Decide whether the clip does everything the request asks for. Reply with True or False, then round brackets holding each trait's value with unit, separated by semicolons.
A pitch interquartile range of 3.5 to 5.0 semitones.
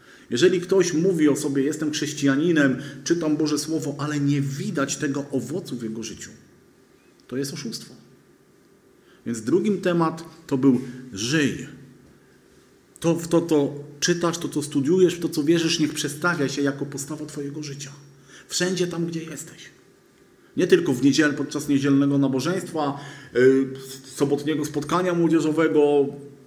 False (2.9 semitones)